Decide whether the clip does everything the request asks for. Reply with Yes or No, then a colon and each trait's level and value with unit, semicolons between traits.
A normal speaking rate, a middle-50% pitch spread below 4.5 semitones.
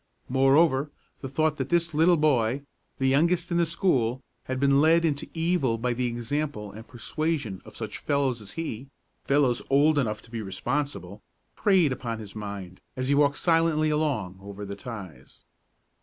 No: average, 170 wpm; wide, 5.5 semitones